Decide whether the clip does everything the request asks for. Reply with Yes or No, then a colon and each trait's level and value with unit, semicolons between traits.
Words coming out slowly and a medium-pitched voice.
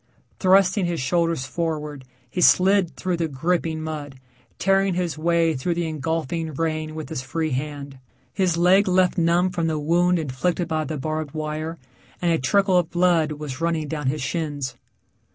No: average, 170 wpm; medium, 165 Hz